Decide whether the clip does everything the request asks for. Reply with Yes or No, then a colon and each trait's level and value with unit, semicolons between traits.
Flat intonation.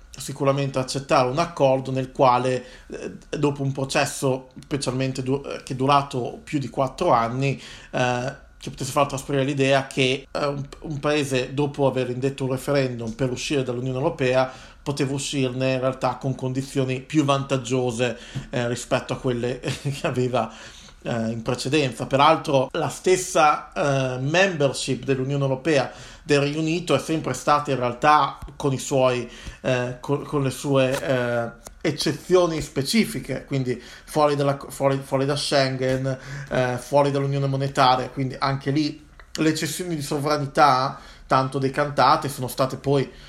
Yes: narrow, 1.9 semitones